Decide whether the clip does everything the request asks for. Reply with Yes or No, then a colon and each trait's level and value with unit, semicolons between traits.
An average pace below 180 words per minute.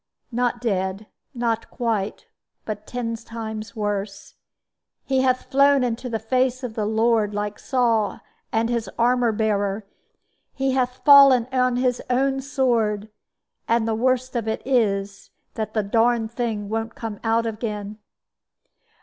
Yes: average, 140 wpm